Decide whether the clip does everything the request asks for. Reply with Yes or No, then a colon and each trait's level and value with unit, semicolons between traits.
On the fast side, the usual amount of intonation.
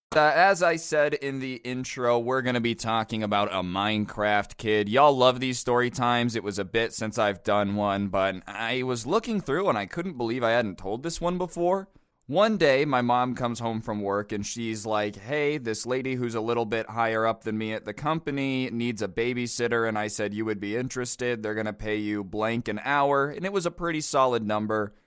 Yes: fast, 225 wpm; average, 3.6 semitones